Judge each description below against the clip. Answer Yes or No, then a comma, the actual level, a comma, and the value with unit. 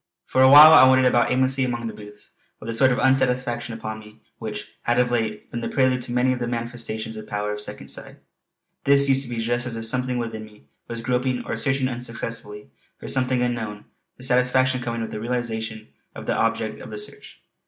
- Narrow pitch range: Yes, narrow, 2.3 semitones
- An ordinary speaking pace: No, fast, 215 wpm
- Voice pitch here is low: Yes, low, 120 Hz